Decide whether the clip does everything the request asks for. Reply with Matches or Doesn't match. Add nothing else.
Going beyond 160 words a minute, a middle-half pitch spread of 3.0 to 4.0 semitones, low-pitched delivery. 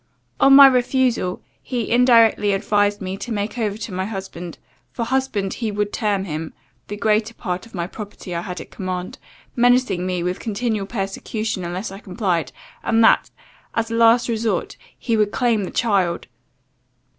Doesn't match